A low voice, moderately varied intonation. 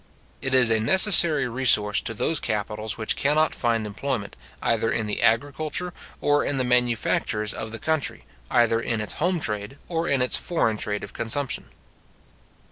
Yes: low, 120 Hz; average, 4.8 semitones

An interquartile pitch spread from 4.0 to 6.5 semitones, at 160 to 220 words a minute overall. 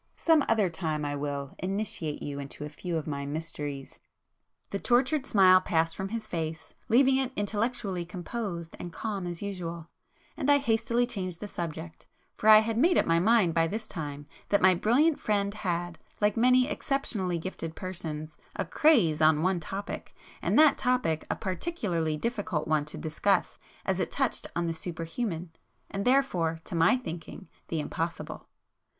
Yes: wide, 5.5 semitones; average, 170 wpm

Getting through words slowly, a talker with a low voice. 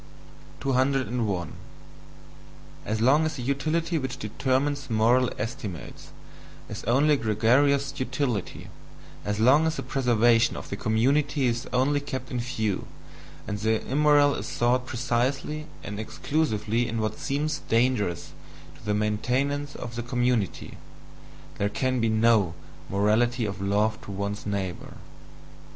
Yes: slow, 130 wpm; low, 120 Hz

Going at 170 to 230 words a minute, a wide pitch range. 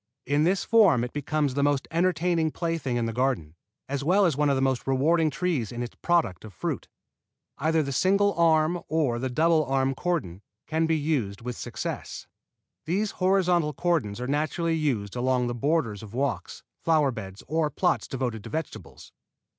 No: average, 180 wpm; average, 4.9 semitones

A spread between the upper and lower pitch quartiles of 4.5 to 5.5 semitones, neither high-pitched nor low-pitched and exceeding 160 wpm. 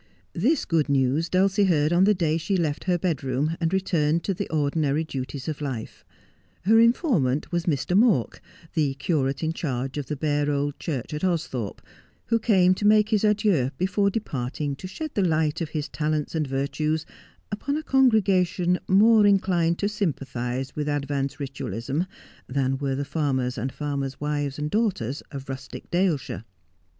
Yes: average, 5.2 semitones; medium, 155 Hz; average, 170 wpm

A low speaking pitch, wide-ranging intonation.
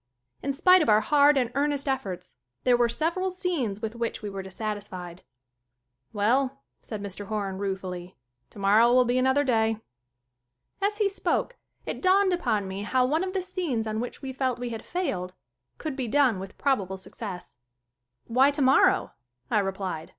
No: high, 240 Hz; wide, 5.9 semitones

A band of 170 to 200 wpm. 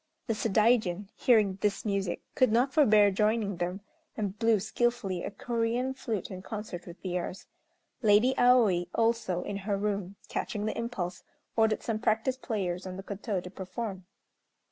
No: average, 155 wpm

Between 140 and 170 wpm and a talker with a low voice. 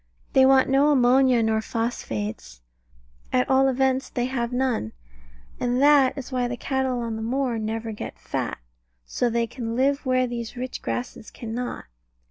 No: average, 160 wpm; high, 245 Hz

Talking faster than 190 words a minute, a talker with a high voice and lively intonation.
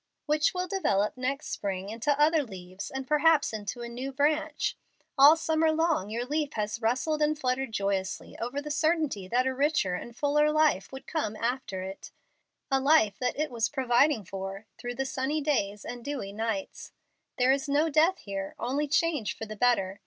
No: average, 180 wpm; very high, 265 Hz; wide, 5.8 semitones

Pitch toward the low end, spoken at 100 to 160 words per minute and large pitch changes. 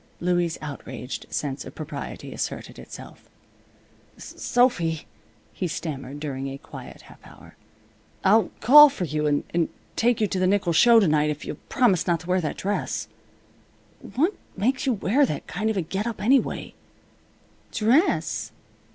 No: medium, 185 Hz; average, 150 wpm; wide, 6.8 semitones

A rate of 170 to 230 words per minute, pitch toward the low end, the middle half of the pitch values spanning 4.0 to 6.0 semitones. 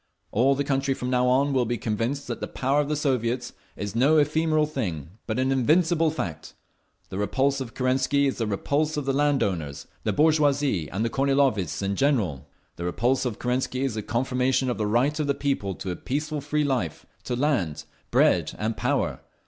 Yes: average, 195 wpm; low, 130 Hz; average, 4.4 semitones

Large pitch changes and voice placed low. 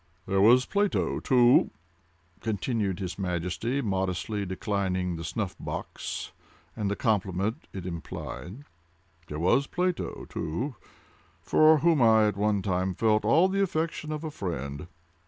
Yes: wide, 5.9 semitones; low, 100 Hz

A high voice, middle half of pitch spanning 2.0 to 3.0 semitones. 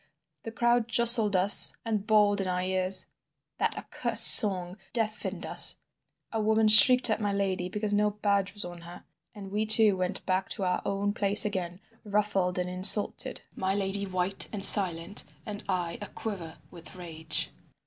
Yes: high, 200 Hz; narrow, 2.4 semitones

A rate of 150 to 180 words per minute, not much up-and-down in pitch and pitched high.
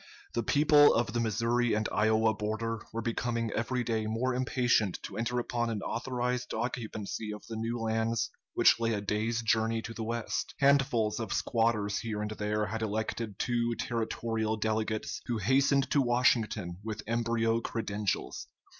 No: average, 160 wpm; narrow, 1.6 semitones; low, 115 Hz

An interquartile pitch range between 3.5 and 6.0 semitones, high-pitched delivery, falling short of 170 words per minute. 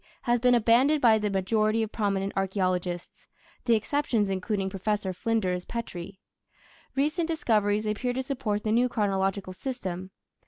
Yes: average, 3.8 semitones; high, 215 Hz; slow, 135 wpm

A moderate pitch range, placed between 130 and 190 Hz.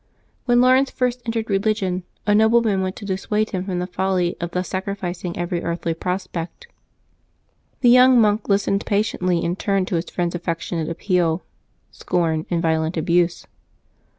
Yes: average, 3.5 semitones; medium, 185 Hz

